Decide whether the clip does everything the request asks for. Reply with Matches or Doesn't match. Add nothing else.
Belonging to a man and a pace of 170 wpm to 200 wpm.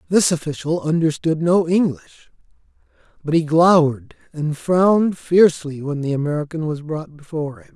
Doesn't match